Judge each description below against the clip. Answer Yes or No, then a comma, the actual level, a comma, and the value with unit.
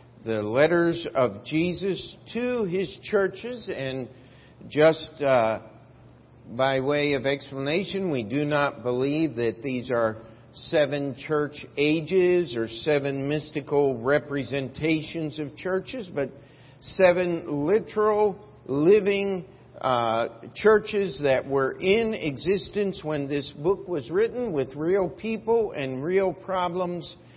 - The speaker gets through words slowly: Yes, slow, 110 wpm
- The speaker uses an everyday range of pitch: No, wide, 5.8 semitones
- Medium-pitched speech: Yes, medium, 150 Hz